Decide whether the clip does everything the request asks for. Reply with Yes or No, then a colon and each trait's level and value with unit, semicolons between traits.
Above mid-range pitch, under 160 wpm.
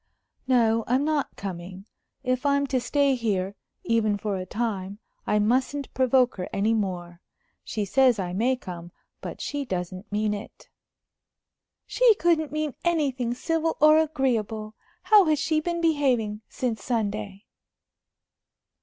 Yes: high, 235 Hz; slow, 135 wpm